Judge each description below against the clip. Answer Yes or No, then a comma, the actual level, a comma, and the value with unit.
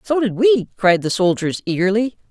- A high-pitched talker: Yes, high, 210 Hz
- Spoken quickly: No, average, 180 wpm